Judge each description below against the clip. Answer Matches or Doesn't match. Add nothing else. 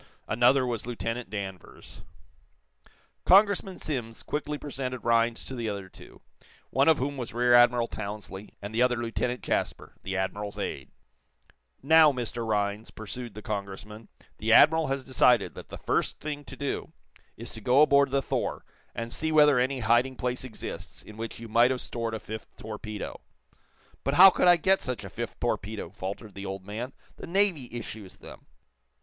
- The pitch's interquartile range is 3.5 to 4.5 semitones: Matches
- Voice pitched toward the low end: Matches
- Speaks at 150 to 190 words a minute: Matches